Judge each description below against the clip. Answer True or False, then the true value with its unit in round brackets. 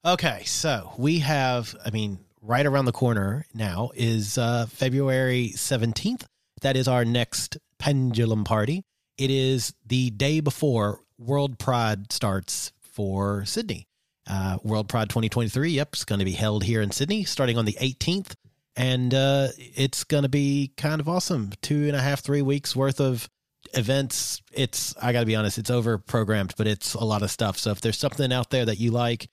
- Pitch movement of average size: True (4.0 semitones)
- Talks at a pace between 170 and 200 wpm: True (180 wpm)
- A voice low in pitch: True (125 Hz)